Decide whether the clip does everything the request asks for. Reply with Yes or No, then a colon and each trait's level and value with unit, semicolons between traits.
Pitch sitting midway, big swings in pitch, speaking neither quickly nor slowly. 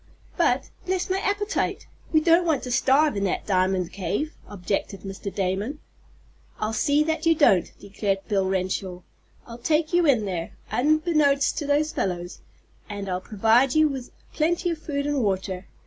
No: high, 245 Hz; wide, 8.1 semitones; average, 165 wpm